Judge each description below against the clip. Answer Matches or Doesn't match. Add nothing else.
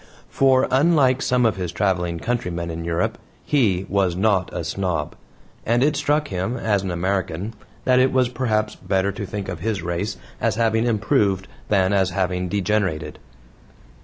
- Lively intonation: Doesn't match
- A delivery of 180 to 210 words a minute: Doesn't match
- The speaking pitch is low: Matches